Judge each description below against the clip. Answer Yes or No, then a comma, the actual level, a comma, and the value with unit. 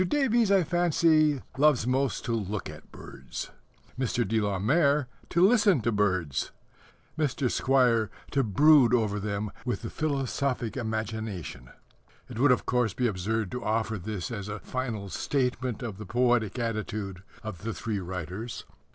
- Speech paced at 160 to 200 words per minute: No, average, 150 wpm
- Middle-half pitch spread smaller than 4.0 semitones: No, average, 4.6 semitones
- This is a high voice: No, low, 115 Hz